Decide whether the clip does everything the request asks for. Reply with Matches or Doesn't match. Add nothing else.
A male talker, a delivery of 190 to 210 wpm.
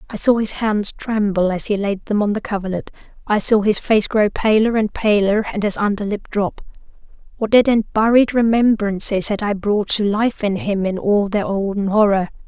Doesn't match